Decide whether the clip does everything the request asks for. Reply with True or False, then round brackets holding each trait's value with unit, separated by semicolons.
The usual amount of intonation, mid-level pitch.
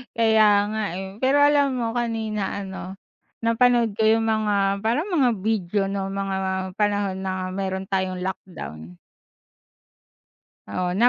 False (3.0 semitones; 205 Hz)